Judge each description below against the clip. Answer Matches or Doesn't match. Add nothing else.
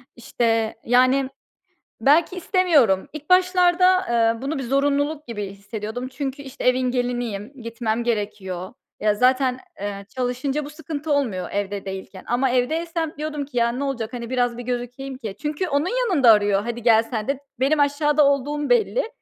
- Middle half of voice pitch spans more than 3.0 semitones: Matches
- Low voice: Doesn't match